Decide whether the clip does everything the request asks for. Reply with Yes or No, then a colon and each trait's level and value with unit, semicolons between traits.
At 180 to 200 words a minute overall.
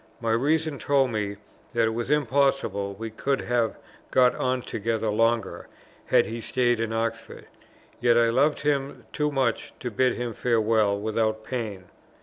No: average, 155 wpm